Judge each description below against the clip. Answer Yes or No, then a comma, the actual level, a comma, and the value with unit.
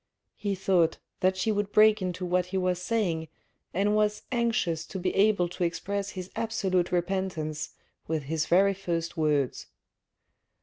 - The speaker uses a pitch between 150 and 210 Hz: Yes, medium, 185 Hz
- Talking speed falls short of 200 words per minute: Yes, average, 150 wpm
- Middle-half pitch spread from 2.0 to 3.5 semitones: Yes, average, 3.0 semitones